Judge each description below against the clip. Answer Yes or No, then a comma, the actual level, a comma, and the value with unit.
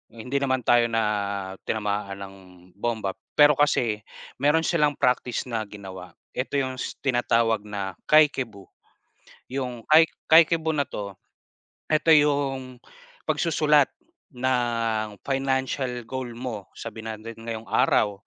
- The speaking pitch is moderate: No, low, 120 Hz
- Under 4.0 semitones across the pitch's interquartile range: No, average, 4.4 semitones